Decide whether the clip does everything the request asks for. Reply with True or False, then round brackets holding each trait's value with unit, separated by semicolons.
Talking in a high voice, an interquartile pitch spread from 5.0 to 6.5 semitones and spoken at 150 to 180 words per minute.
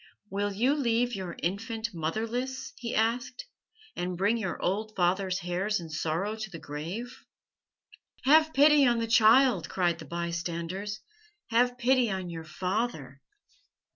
False (210 Hz; 5.4 semitones; 140 wpm)